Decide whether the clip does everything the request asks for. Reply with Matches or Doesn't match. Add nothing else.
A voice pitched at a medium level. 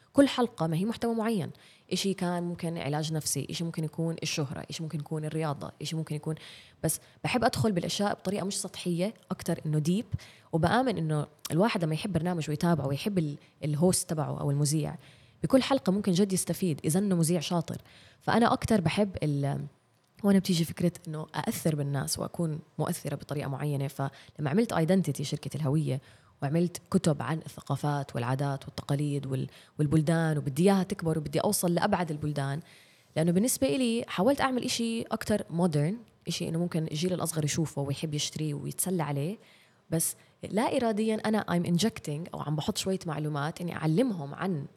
Matches